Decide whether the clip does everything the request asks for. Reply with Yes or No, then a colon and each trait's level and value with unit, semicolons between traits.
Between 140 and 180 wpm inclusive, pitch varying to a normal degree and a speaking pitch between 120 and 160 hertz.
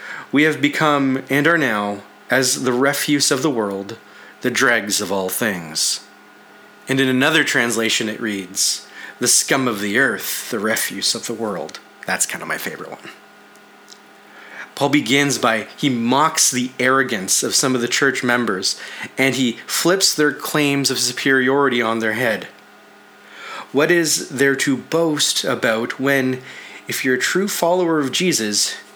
Yes: average, 155 wpm; average, 3.9 semitones; low, 135 Hz